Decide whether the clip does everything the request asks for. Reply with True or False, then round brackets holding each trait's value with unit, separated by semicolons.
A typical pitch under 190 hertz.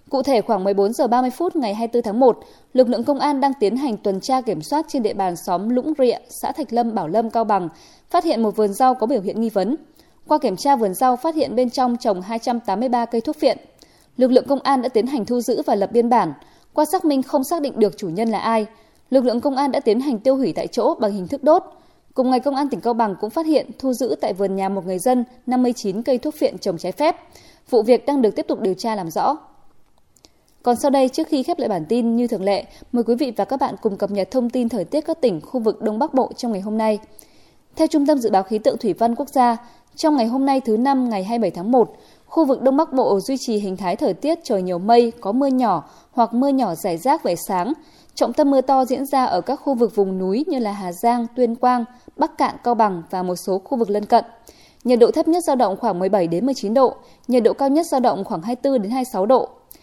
False (245 Hz)